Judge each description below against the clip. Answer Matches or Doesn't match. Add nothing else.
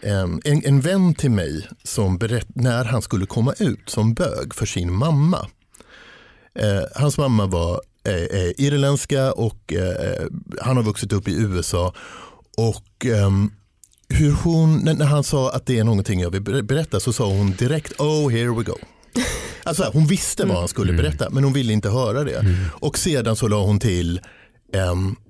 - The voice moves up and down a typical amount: Doesn't match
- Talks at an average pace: Matches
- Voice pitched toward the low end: Matches